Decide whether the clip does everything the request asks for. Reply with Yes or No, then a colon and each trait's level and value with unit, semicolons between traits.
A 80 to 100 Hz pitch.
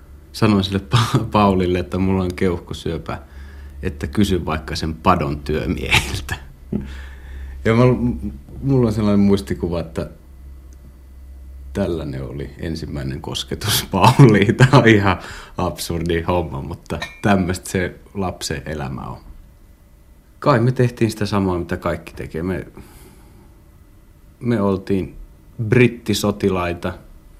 Yes: very low, 90 Hz